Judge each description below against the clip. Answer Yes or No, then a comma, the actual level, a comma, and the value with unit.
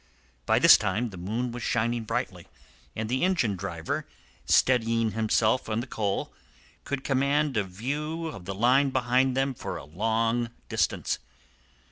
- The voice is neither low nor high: No, low, 120 Hz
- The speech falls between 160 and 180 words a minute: No, average, 150 wpm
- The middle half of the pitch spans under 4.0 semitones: Yes, average, 3.4 semitones